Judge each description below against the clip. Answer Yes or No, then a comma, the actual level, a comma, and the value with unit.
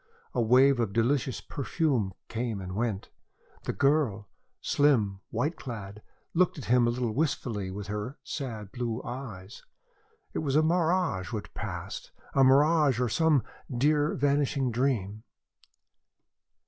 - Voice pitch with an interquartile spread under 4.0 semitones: No, average, 4.9 semitones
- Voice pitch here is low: Yes, low, 125 Hz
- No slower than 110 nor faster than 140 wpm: Yes, slow, 135 wpm